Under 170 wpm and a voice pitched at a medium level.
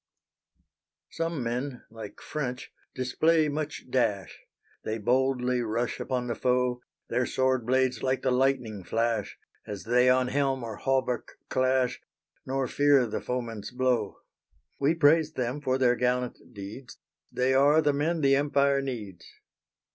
No: average, 140 wpm; low, 125 Hz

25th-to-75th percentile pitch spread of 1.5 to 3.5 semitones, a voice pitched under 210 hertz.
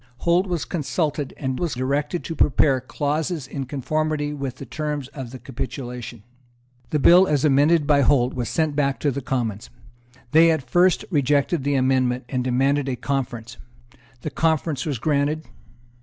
Yes: average, 3.0 semitones; medium, 140 Hz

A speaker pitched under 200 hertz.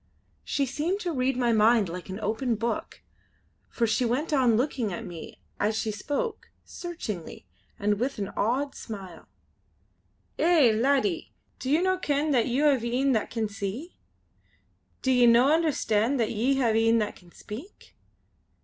No: high, 240 Hz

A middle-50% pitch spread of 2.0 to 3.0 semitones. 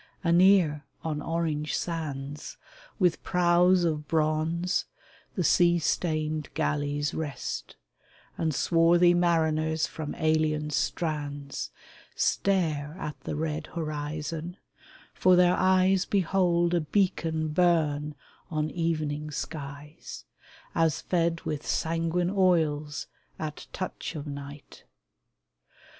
Yes: narrow, 2.5 semitones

